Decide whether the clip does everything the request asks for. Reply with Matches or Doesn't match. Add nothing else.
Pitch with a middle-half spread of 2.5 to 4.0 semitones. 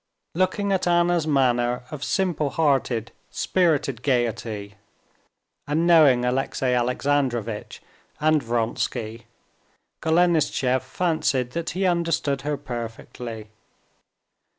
Doesn't match